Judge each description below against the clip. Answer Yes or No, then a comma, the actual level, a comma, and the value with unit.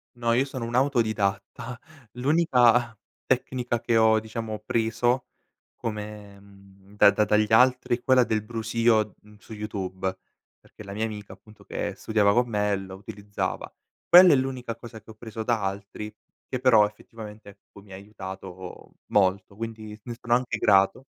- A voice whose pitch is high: No, low, 110 Hz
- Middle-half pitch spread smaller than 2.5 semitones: No, average, 2.8 semitones